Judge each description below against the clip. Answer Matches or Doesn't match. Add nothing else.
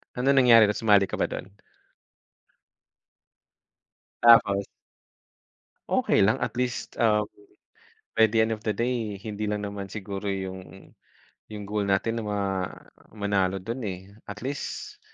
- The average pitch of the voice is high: Doesn't match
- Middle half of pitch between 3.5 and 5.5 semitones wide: Doesn't match